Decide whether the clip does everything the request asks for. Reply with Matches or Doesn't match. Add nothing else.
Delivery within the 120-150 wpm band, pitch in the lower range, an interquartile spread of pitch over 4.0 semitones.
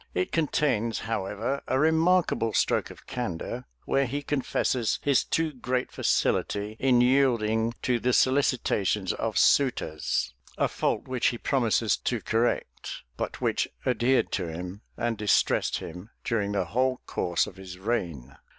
Matches